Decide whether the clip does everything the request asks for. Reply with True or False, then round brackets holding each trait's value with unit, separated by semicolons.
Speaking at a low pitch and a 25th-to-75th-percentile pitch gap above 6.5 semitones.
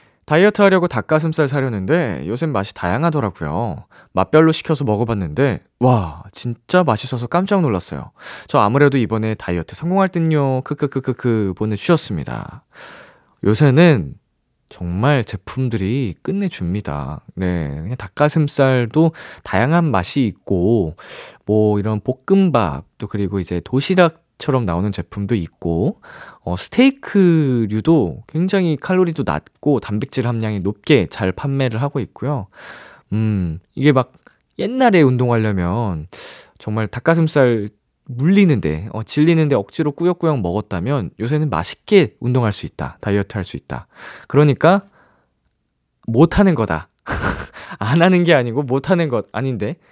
True (125 Hz; 7.4 semitones)